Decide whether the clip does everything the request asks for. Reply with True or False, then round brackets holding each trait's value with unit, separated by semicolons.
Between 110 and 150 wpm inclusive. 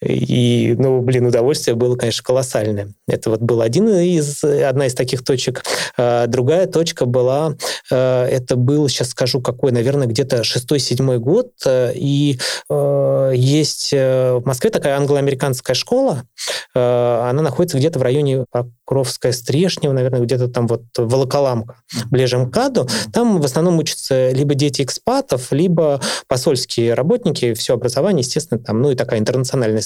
True (135 wpm)